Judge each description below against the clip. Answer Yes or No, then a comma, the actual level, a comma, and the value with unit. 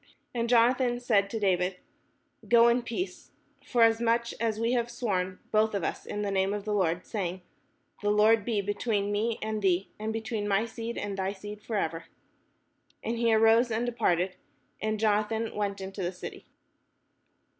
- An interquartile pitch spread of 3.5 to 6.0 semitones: No, narrow, 2.6 semitones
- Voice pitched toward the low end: No, high, 215 Hz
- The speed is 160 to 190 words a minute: Yes, average, 175 wpm